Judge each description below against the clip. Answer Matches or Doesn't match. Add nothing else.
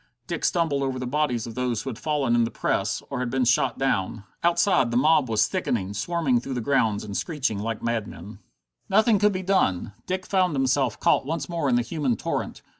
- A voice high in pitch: Doesn't match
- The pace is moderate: Doesn't match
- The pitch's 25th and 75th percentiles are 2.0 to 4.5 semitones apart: Doesn't match